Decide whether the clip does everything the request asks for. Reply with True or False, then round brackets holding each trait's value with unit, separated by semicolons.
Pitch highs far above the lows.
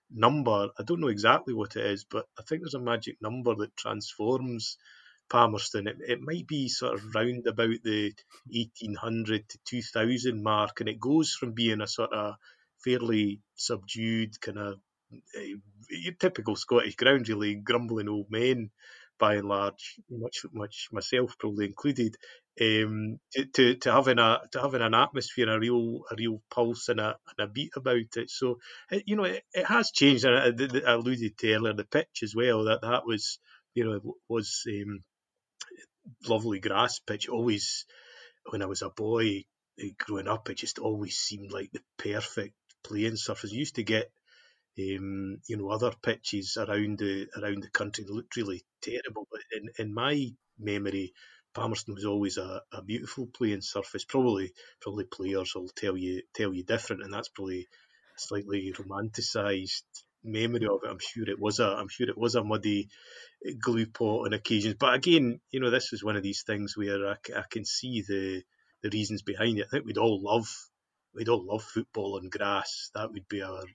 False (2.9 semitones)